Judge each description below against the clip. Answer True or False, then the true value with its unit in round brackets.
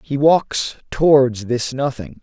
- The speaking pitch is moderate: False (130 Hz)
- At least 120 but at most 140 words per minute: True (135 wpm)